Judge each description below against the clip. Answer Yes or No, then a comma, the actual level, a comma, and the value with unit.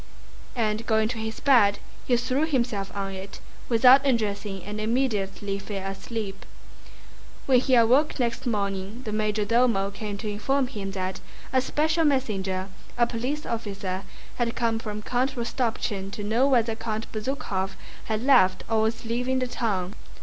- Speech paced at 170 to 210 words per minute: No, average, 155 wpm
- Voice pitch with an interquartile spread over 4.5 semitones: No, average, 3.8 semitones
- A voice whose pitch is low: No, high, 225 Hz